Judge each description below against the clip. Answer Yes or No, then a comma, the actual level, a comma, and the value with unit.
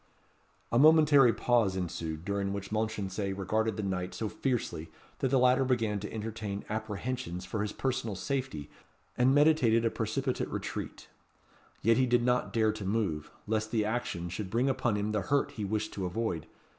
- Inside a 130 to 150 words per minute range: No, average, 170 wpm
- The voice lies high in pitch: No, low, 110 Hz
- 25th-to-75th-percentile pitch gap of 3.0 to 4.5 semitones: Yes, average, 3.7 semitones